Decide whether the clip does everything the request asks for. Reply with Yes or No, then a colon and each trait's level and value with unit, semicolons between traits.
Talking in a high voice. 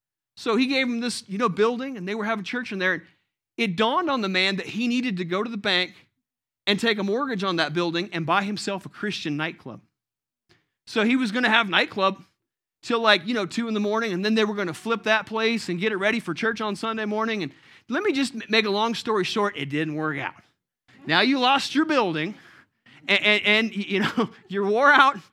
Yes: high, 210 Hz